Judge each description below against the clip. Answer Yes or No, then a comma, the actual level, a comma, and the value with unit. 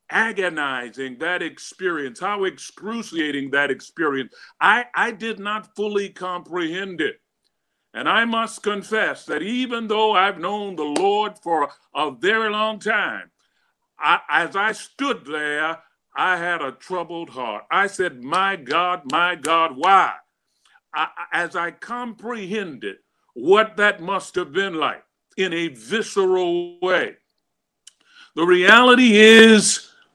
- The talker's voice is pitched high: Yes, high, 200 Hz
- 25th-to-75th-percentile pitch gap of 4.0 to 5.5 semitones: Yes, average, 4.4 semitones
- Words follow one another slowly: Yes, slow, 125 wpm